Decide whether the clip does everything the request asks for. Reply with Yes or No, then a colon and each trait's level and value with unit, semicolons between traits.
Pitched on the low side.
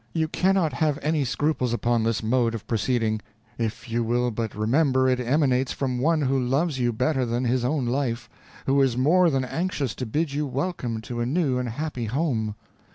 Yes: low, 130 Hz